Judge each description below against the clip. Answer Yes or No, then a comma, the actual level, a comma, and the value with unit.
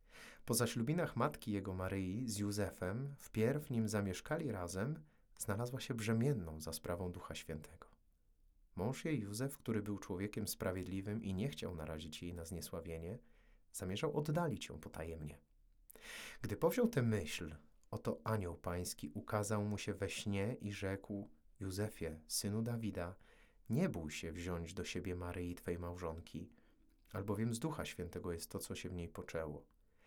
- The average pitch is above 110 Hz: No, very low, 95 Hz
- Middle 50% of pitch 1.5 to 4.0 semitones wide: No, average, 4.7 semitones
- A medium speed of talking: Yes, average, 145 wpm